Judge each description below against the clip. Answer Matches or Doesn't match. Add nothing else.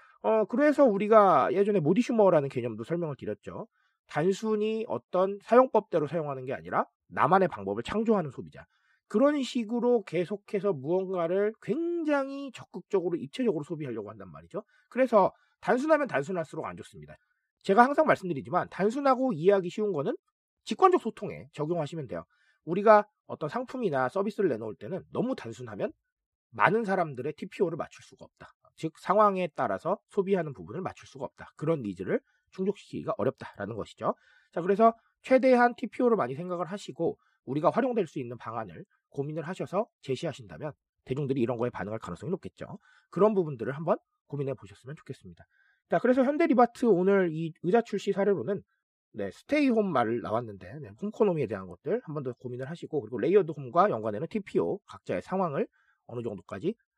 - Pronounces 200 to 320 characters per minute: Doesn't match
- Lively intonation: Matches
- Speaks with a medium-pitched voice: Doesn't match